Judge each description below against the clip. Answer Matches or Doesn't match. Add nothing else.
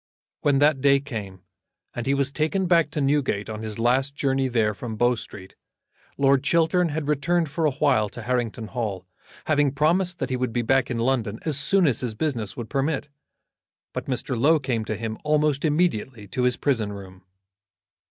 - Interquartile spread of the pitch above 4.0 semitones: Matches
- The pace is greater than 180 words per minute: Matches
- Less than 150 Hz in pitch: Matches